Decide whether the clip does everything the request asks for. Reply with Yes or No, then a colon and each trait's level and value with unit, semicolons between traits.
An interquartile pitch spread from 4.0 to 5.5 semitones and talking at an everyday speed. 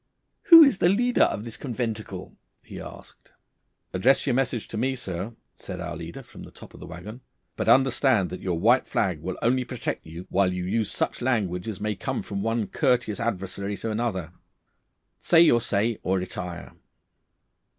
Yes: average, 5.0 semitones; average, 180 wpm